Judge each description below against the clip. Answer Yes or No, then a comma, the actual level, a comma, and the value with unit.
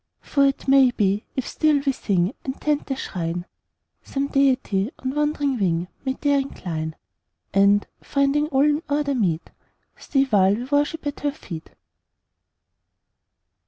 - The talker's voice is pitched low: No, very high, 265 Hz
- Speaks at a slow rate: No, average, 145 wpm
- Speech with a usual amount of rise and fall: No, wide, 6.4 semitones